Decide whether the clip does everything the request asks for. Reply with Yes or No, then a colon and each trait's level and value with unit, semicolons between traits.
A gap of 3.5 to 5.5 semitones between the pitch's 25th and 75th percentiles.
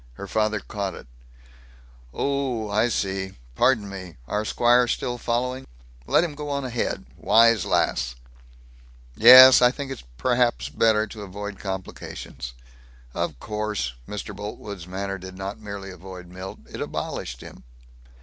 Yes: average, 4.0 semitones